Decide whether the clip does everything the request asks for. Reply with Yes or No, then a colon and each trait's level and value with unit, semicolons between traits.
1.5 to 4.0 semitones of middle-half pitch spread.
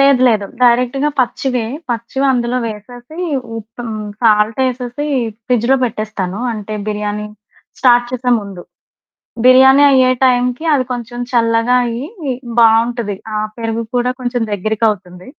Yes: average, 2.8 semitones